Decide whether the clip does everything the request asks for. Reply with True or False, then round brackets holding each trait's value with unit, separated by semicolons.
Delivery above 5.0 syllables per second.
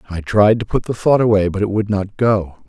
True (5.4 syllables/s)